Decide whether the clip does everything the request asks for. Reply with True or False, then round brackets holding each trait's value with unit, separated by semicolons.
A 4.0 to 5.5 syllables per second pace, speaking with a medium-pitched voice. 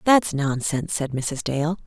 True (4.2 syllables/s; 150 Hz)